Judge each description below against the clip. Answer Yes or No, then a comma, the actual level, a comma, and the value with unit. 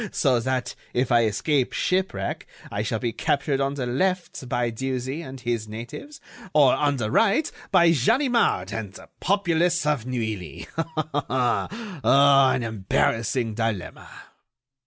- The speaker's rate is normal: No, slow, 130 wpm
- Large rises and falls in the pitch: Yes, wide, 5.9 semitones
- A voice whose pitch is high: No, low, 130 Hz